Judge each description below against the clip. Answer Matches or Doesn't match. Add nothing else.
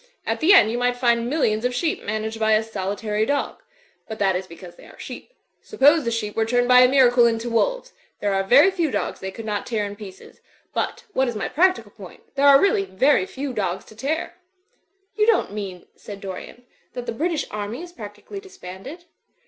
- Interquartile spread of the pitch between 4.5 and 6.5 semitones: Matches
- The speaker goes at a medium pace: Doesn't match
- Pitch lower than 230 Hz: Doesn't match